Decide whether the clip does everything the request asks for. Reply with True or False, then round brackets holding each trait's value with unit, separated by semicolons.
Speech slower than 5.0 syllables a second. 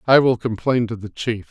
False (5.2 syllables/s)